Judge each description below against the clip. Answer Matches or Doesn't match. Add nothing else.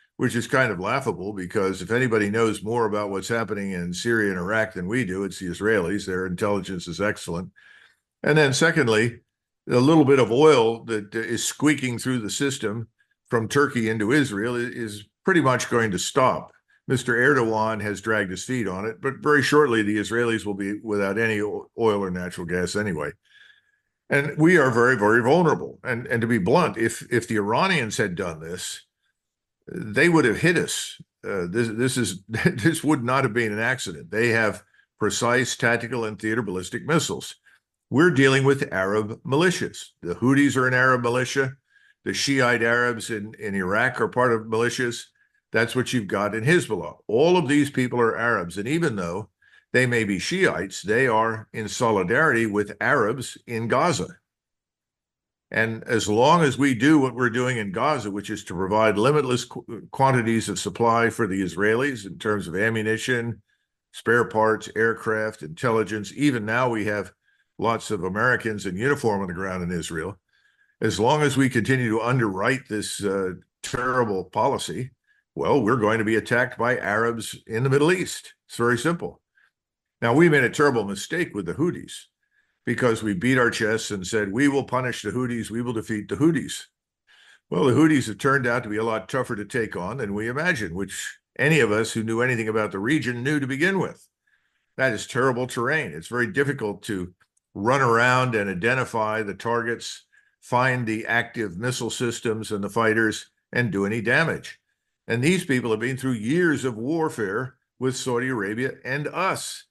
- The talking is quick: Doesn't match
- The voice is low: Matches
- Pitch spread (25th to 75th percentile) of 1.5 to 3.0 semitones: Doesn't match